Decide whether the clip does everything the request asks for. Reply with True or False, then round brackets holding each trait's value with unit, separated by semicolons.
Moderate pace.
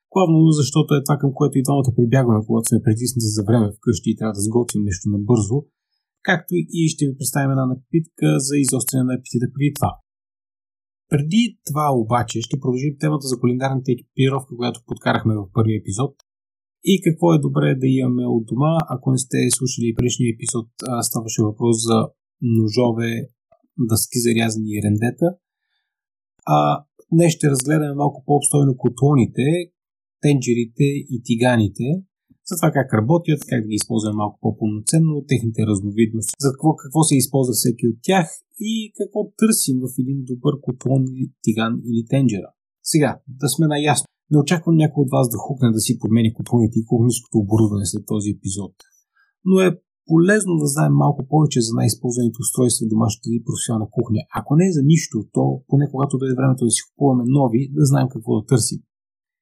False (170 wpm)